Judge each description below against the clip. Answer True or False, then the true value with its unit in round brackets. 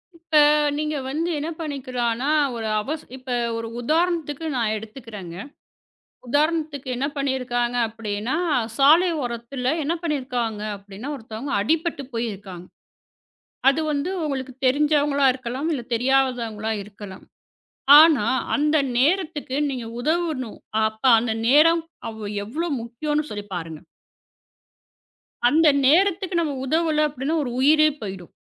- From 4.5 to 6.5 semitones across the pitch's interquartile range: True (5.1 semitones)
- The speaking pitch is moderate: False (265 Hz)